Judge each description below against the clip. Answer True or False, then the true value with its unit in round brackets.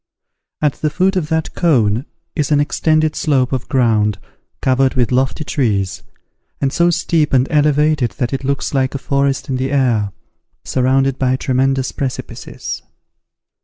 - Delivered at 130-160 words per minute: True (150 wpm)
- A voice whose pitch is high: False (135 Hz)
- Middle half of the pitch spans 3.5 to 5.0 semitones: False (2.7 semitones)